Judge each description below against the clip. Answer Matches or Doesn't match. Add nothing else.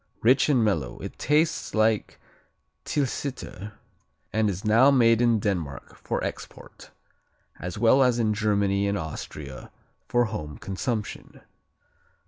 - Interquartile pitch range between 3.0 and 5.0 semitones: Matches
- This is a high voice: Doesn't match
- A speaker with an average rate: Doesn't match